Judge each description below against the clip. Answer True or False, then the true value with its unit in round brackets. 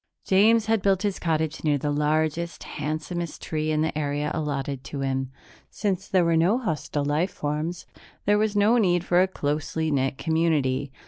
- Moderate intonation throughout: True (3.9 semitones)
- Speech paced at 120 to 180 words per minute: True (175 wpm)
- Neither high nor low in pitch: True (160 Hz)